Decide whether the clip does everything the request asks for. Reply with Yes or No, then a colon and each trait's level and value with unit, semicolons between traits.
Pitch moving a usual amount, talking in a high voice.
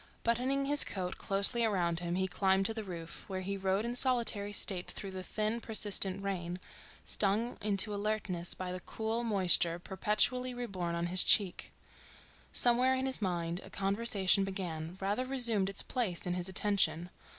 Yes: average, 3.6 semitones; high, 195 Hz